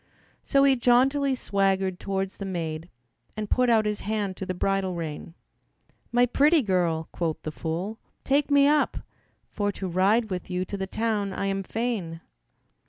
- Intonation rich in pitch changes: No, average, 4.7 semitones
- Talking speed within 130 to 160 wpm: No, average, 170 wpm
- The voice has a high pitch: Yes, high, 195 Hz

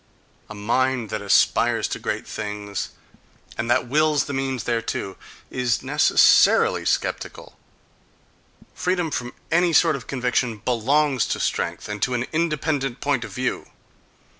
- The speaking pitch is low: Yes, low, 125 Hz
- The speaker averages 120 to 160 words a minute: Yes, slow, 135 wpm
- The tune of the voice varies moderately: Yes, average, 4.2 semitones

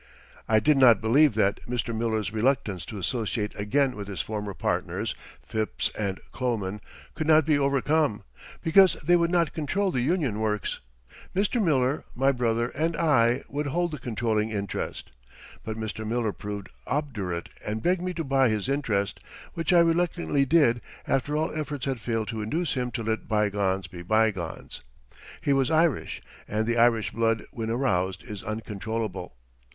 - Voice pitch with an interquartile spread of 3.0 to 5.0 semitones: No, wide, 5.5 semitones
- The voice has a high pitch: No, low, 115 Hz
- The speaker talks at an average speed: Yes, average, 165 wpm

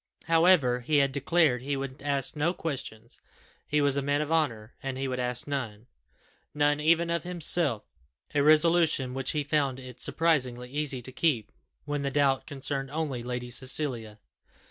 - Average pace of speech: Yes, average, 165 wpm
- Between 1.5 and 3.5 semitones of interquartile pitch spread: Yes, average, 3.2 semitones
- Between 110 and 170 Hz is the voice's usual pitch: Yes, medium, 140 Hz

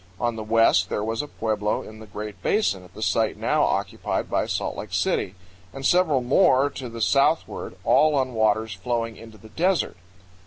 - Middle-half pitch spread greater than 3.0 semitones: Yes, average, 4.3 semitones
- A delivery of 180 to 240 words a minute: Yes, average, 190 wpm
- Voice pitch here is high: No, low, 115 Hz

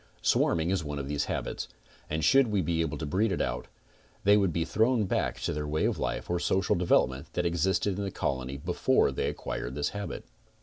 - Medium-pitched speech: No, very low, 85 Hz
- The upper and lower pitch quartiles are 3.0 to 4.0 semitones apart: No, average, 4.9 semitones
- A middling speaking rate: No, fast, 215 wpm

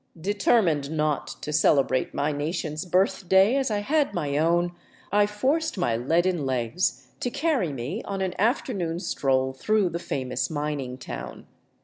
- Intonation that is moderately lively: No, wide, 6.1 semitones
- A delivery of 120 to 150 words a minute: Yes, average, 145 wpm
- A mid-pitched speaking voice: Yes, medium, 170 Hz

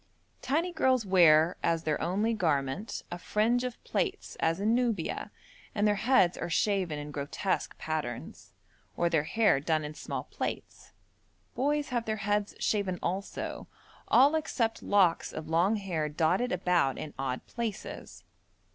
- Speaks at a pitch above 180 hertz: Yes, high, 190 Hz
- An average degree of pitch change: No, wide, 6.0 semitones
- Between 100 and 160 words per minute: Yes, average, 145 wpm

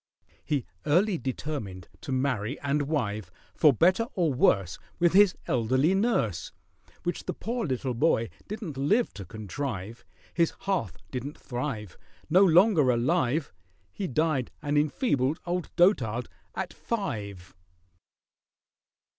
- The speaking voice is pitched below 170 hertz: Yes, medium, 140 Hz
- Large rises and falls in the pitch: Yes, wide, 6.9 semitones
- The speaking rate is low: Yes, slow, 120 wpm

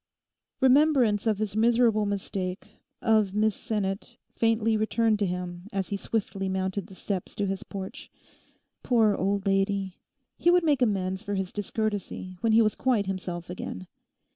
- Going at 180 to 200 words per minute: No, average, 155 wpm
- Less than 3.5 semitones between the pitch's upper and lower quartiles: Yes, narrow, 2.6 semitones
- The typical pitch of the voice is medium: No, high, 205 Hz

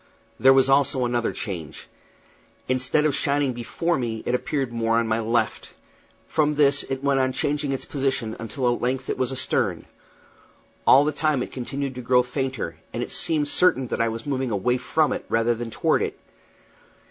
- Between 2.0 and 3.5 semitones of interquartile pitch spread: Yes, average, 2.9 semitones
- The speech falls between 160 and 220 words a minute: Yes, average, 185 wpm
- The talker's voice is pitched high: No, low, 130 Hz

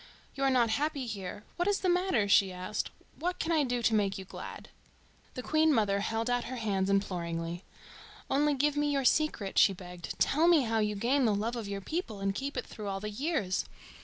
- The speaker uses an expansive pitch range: Yes, wide, 6.3 semitones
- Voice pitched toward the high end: Yes, high, 225 Hz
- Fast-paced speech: Yes, fast, 220 wpm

